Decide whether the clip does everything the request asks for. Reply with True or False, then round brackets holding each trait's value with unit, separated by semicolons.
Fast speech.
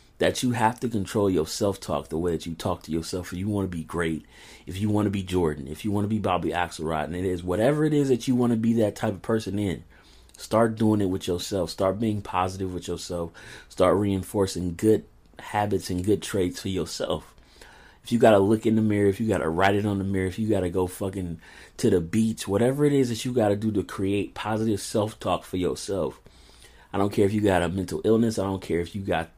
True (255 wpm)